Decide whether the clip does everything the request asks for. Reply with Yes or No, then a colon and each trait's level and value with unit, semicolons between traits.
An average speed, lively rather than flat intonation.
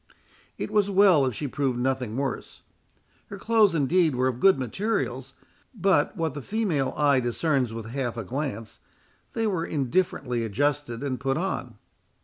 Yes: average, 155 wpm; wide, 6.4 semitones